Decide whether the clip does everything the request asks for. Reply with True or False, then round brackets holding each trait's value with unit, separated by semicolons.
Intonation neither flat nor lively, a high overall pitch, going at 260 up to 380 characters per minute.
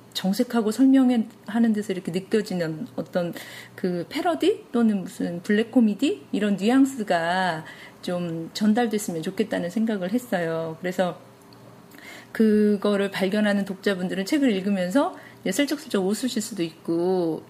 True (4.3 semitones; 205 Hz; 295 characters per minute)